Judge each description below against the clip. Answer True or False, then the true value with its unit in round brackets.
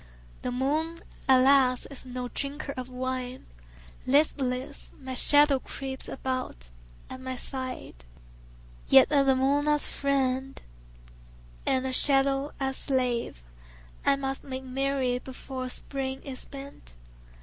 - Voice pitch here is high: True (265 Hz)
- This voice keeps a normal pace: False (125 wpm)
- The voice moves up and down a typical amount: False (1.4 semitones)